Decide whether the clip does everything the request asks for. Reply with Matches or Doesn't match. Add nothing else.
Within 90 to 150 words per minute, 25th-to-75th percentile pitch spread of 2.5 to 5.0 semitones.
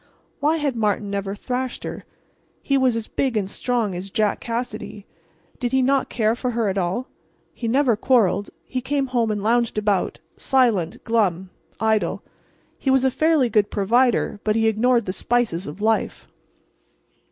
Doesn't match